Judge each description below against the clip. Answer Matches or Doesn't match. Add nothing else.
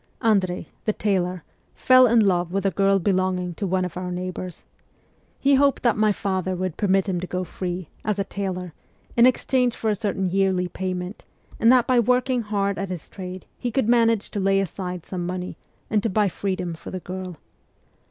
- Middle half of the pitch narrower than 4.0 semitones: Matches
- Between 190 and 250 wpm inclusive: Matches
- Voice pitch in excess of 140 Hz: Matches